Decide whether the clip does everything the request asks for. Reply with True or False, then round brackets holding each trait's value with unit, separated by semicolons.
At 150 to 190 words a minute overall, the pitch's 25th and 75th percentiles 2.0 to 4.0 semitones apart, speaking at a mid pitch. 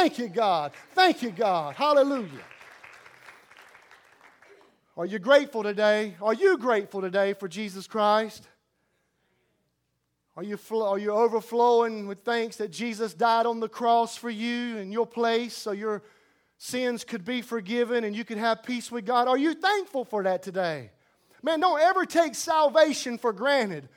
False (155 wpm; 2.8 semitones; 230 Hz)